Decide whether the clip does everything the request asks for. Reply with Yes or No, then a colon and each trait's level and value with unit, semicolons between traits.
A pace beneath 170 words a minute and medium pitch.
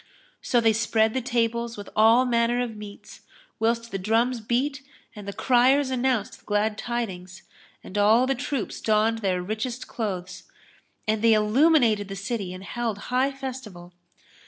No: average, 160 wpm; high, 225 Hz